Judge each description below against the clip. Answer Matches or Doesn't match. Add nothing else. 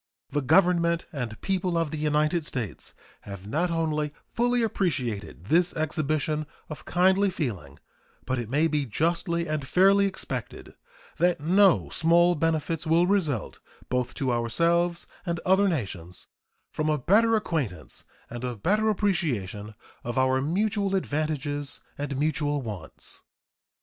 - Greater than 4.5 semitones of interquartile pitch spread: Matches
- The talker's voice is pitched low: Doesn't match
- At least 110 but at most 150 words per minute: Matches